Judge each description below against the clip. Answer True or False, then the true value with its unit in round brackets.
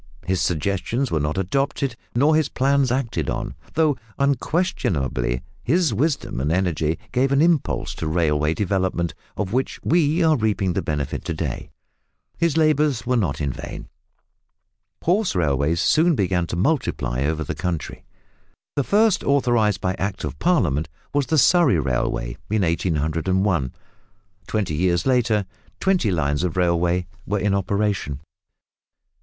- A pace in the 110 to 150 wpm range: True (140 wpm)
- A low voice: True (100 Hz)